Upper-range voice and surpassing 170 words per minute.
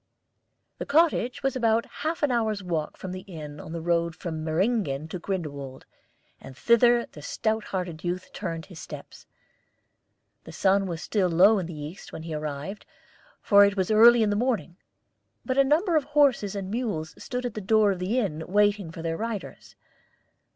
Yes: high, 195 Hz; average, 185 wpm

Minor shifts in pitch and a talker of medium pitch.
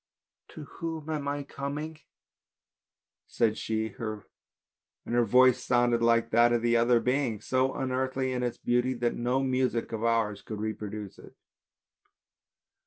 No: narrow, 2.3 semitones; low, 120 Hz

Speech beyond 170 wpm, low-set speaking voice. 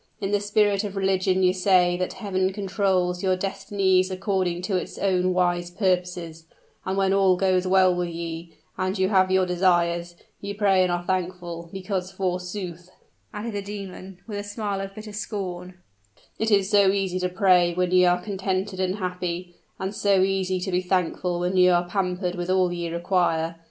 No: average, 180 wpm; medium, 185 Hz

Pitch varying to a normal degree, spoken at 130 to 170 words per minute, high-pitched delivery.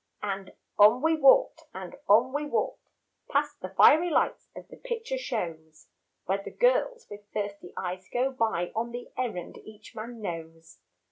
No: wide, 7.4 semitones; average, 160 wpm; high, 220 Hz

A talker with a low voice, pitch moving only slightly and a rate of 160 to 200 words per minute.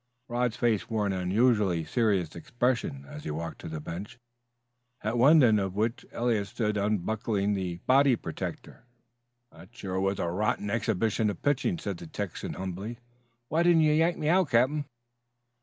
No: low, 105 Hz; average, 4.6 semitones; average, 170 wpm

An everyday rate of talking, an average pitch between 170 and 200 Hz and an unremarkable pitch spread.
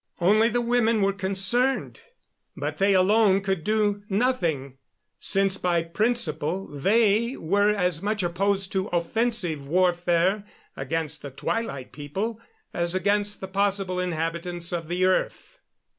No: slow, 130 wpm; high, 190 Hz; average, 3.5 semitones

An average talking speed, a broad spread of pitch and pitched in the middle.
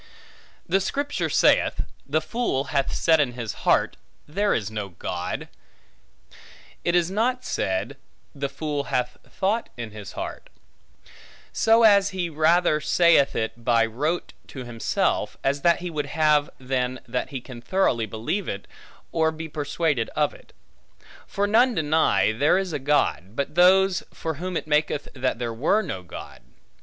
Yes: average, 155 wpm; wide, 6.3 semitones; medium, 150 Hz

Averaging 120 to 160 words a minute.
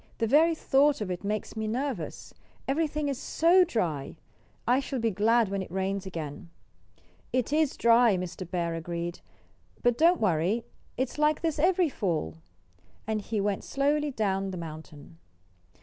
Yes: average, 150 wpm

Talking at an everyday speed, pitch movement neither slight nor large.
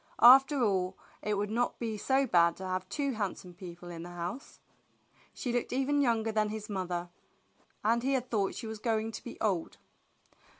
Yes: average, 185 wpm; average, 4.7 semitones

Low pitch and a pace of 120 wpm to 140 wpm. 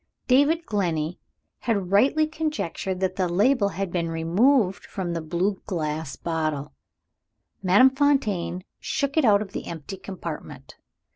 No: high, 190 Hz; slow, 135 wpm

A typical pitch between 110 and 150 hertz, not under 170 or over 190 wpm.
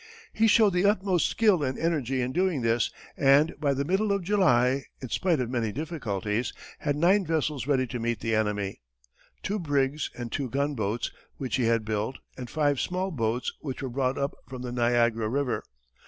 Yes: low, 135 Hz; average, 185 wpm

